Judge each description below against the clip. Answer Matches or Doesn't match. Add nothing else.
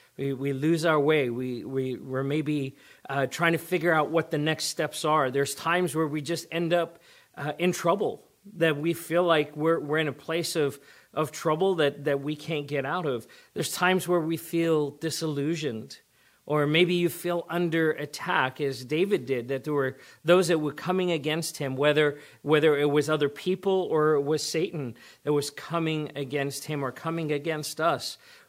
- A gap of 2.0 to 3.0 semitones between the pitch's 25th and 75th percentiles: Matches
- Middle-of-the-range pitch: Matches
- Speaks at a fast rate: Doesn't match